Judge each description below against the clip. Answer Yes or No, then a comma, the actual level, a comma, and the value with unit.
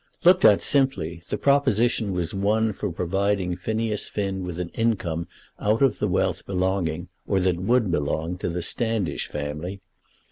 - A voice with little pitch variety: No, average, 4.0 semitones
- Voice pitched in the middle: No, very low, 95 Hz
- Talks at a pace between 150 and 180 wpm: Yes, average, 155 wpm